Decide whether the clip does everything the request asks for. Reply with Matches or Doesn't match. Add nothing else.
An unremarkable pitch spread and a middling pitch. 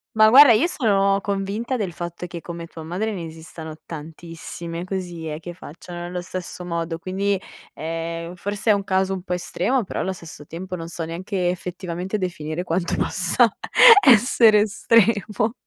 Matches